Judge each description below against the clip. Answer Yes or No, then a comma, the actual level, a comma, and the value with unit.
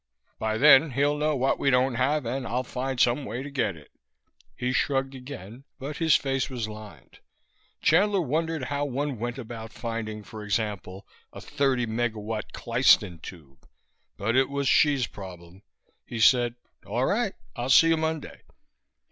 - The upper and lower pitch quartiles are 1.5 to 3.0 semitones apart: No, average, 4.4 semitones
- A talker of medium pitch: No, low, 125 Hz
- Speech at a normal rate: Yes, average, 160 wpm